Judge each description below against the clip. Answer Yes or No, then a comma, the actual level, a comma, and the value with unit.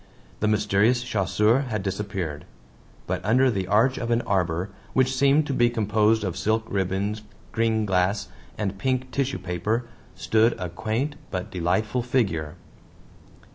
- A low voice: Yes, low, 110 Hz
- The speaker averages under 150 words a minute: Yes, average, 140 wpm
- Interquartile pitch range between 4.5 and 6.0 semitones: No, average, 4.0 semitones